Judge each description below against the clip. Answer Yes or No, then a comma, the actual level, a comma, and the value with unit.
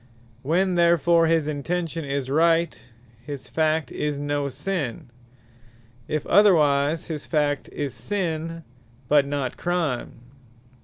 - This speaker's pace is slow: Yes, slow, 110 wpm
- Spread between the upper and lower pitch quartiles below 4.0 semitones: Yes, average, 2.9 semitones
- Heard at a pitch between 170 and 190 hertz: No, medium, 155 Hz